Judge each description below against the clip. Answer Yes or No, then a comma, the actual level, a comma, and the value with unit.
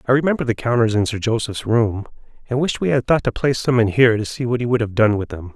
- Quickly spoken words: Yes, fast, 290 wpm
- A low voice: Yes, low, 115 Hz